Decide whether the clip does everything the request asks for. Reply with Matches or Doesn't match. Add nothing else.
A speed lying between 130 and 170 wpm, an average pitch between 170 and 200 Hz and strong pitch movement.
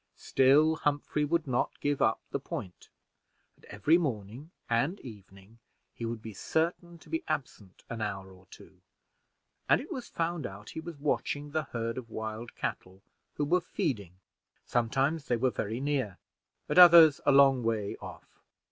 Doesn't match